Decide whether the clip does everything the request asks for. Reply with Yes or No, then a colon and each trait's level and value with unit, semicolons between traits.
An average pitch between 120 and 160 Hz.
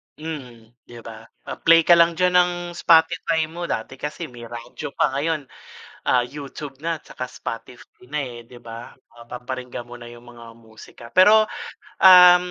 Yes: low, 135 Hz